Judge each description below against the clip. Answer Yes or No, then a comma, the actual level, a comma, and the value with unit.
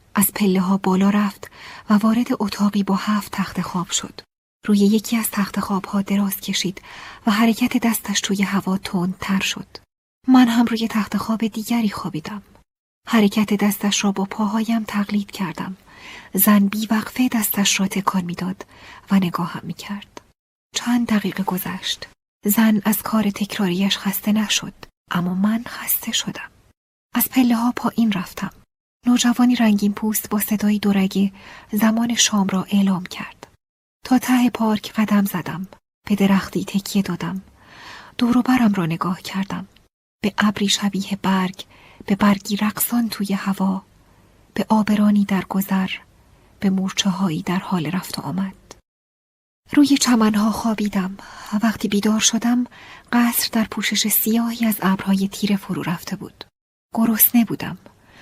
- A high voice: Yes, high, 205 Hz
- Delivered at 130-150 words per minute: Yes, average, 140 wpm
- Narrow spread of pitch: Yes, narrow, 2.3 semitones